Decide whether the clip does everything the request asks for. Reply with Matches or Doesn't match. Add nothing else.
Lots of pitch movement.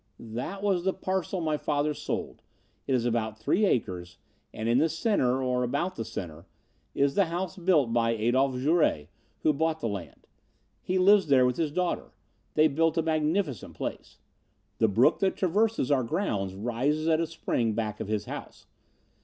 Matches